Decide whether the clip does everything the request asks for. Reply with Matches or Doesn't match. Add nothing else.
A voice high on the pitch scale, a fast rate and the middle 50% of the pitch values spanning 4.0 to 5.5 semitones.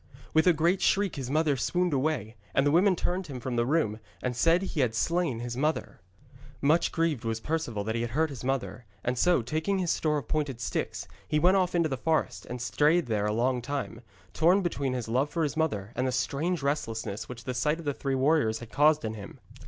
Doesn't match